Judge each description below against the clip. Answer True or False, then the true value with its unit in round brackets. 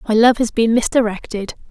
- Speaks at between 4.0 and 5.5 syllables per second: False (5.8 syllables/s)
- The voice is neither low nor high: False (225 Hz)